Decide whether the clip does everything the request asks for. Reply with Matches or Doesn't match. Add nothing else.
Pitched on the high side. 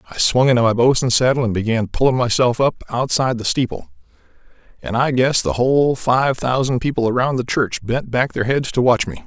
Doesn't match